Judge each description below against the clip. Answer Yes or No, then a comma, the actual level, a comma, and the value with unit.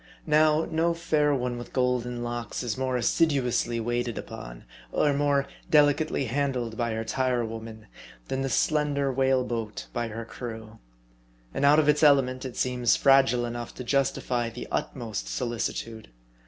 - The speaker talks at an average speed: Yes, average, 155 wpm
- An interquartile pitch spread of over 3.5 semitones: No, average, 3.1 semitones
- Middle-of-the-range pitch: No, low, 125 Hz